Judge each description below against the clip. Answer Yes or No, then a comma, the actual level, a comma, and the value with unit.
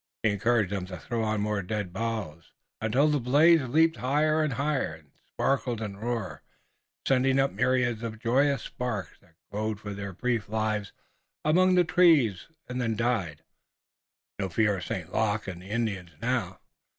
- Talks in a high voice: No, low, 115 Hz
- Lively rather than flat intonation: No, average, 4.4 semitones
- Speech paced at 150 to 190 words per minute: Yes, average, 165 wpm